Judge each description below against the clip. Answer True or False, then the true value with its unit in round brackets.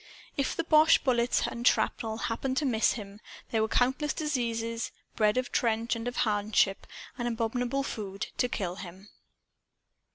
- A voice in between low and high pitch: False (230 Hz)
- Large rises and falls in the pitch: False (2.7 semitones)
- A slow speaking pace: False (160 wpm)